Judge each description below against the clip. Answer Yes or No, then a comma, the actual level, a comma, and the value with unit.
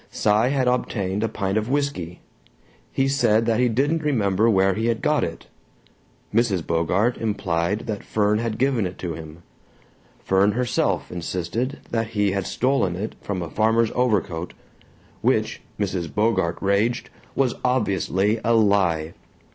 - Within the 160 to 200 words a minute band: No, average, 145 wpm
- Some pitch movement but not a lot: Yes, average, 3.7 semitones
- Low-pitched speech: Yes, low, 105 Hz